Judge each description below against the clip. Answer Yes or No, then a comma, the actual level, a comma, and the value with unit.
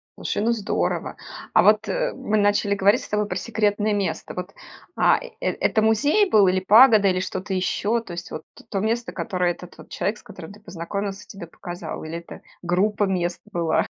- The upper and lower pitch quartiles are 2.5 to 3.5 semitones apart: Yes, average, 2.9 semitones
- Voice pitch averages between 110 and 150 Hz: No, high, 200 Hz